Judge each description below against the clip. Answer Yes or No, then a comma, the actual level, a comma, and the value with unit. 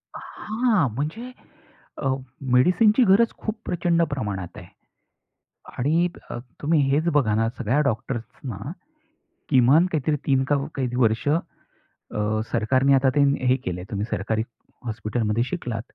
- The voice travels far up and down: Yes, wide, 6.4 semitones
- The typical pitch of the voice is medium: No, low, 130 Hz